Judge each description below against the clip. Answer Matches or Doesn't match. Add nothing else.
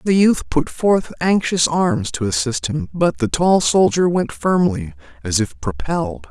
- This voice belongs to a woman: Doesn't match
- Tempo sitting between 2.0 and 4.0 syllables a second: Doesn't match